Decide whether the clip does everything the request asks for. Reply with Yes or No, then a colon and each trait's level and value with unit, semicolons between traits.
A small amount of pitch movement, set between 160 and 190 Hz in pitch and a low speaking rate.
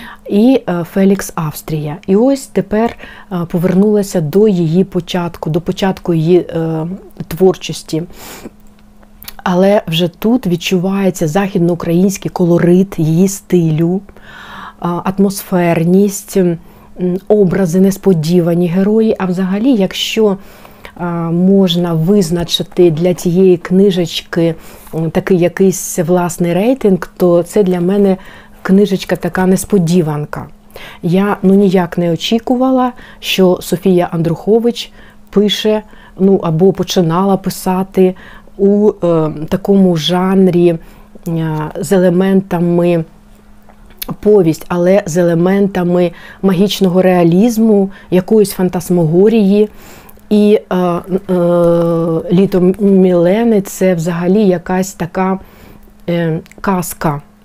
Yes: narrow, 2.2 semitones; medium, 185 Hz; slow, 90 wpm